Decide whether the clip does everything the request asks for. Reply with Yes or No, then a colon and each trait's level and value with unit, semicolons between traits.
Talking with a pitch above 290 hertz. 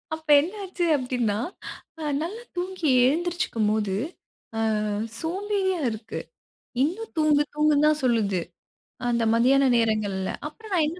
Yes: very high, 300 Hz